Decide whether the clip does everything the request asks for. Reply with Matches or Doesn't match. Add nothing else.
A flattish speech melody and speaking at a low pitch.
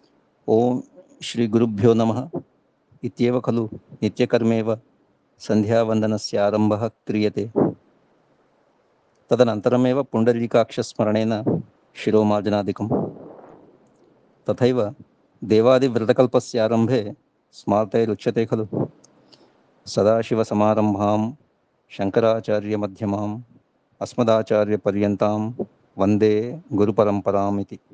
Matches